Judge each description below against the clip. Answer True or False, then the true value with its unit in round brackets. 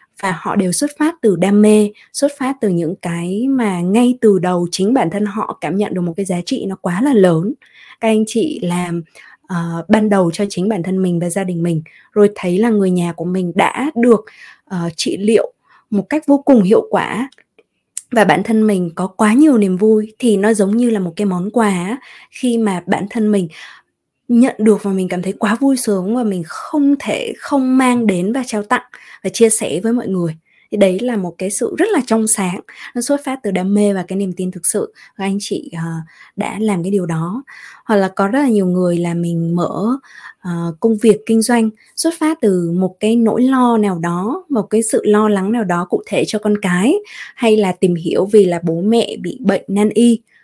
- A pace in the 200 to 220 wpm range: False (230 wpm)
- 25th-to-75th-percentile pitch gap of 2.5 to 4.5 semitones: True (3.9 semitones)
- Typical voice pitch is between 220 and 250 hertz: False (210 Hz)